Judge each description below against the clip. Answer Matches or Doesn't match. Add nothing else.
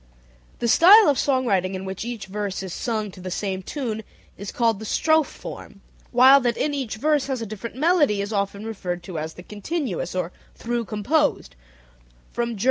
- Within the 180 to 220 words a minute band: Matches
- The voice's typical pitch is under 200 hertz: Doesn't match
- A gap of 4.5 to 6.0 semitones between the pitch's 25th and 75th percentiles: Matches